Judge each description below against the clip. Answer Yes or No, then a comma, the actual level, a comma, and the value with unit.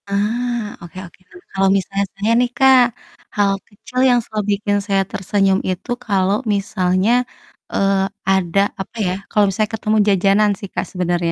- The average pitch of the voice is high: Yes, high, 200 Hz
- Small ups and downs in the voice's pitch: Yes, narrow, 2.0 semitones